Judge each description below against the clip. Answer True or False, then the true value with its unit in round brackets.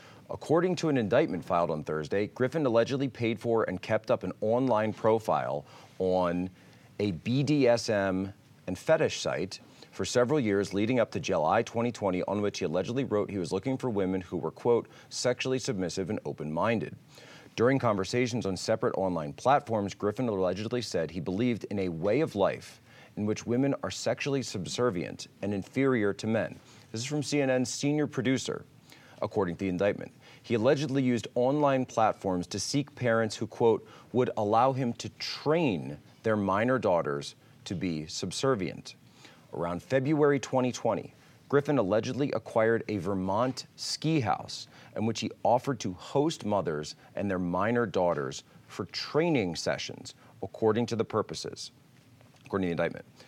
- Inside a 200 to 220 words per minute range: False (155 wpm)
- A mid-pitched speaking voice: False (115 Hz)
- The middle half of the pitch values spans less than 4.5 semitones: False (5.1 semitones)